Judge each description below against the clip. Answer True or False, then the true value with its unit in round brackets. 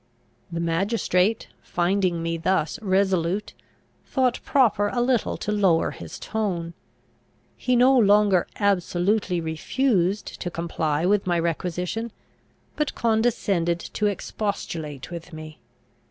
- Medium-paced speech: False (110 wpm)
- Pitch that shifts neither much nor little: True (4.0 semitones)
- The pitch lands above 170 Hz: True (190 Hz)